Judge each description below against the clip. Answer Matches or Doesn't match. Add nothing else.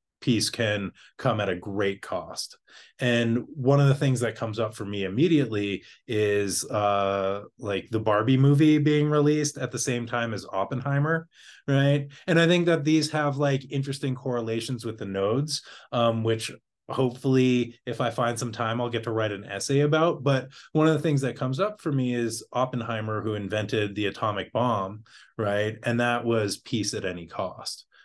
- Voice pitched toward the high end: Doesn't match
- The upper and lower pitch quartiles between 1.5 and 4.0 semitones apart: Doesn't match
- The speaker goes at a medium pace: Matches